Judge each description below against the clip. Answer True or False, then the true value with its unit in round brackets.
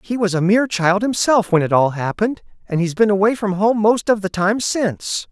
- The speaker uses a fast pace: True (235 wpm)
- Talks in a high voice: True (200 Hz)